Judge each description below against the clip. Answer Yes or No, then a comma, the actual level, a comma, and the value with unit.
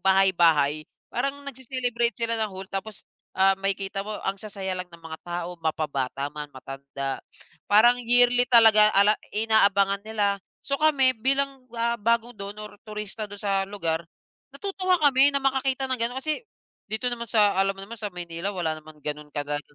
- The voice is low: No, high, 205 Hz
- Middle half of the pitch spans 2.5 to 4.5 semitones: No, average, 5.2 semitones